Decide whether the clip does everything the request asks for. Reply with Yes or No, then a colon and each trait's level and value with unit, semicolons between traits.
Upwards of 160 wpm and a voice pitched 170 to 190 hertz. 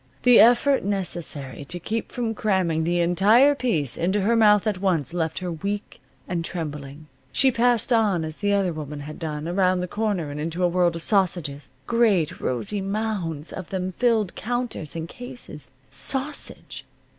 Yes: average, 170 wpm; medium, 185 Hz